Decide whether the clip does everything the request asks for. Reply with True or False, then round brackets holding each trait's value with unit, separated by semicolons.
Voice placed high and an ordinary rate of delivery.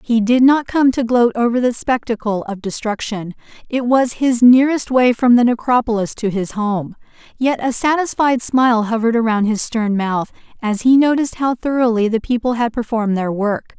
True (235 Hz; 185 wpm)